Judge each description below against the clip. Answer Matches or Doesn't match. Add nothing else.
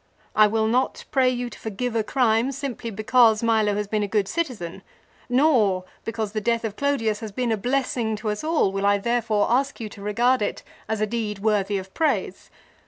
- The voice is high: Matches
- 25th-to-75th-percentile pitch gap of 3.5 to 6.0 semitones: Doesn't match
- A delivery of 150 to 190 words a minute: Doesn't match